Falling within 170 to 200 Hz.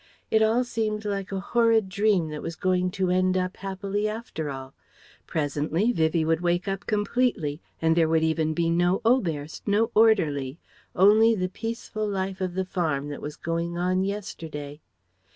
Yes: medium, 185 Hz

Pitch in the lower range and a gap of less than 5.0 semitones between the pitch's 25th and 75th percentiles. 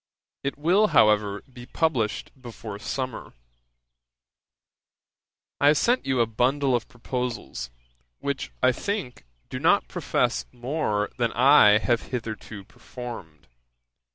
Yes: low, 120 Hz; average, 4.2 semitones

